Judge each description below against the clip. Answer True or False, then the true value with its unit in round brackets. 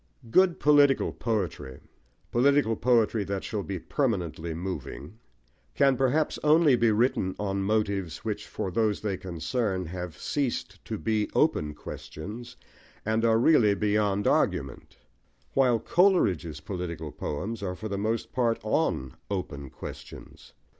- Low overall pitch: True (105 Hz)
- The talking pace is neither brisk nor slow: False (130 wpm)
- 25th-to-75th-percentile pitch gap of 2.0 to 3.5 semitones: False (4.7 semitones)